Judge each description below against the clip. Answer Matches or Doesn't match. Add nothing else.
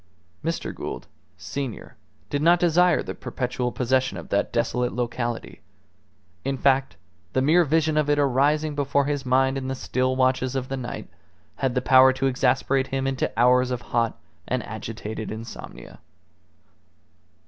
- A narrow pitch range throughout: Matches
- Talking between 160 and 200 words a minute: Doesn't match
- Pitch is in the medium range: Doesn't match